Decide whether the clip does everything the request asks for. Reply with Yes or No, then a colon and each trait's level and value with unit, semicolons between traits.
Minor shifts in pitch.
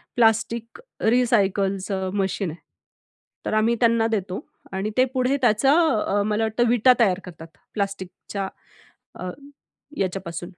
No: average, 3.5 semitones